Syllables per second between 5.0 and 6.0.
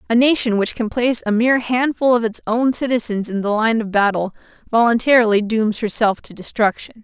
Yes: 5.6 syllables/s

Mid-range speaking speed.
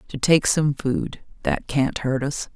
Yes: average, 190 wpm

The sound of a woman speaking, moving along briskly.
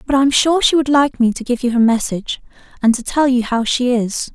Yes: female; fast, 275 wpm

